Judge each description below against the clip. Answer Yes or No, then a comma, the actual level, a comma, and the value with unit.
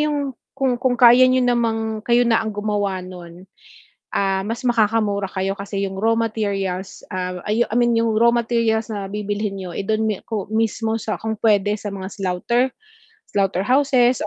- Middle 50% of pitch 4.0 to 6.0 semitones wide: No, average, 3.1 semitones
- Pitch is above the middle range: Yes, high, 220 Hz